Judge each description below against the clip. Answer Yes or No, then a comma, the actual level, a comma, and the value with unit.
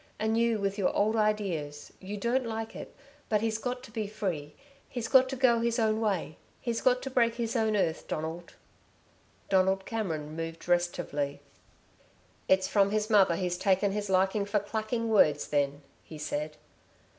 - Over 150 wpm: Yes, average, 170 wpm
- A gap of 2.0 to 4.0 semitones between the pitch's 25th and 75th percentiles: No, average, 4.4 semitones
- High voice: Yes, high, 205 Hz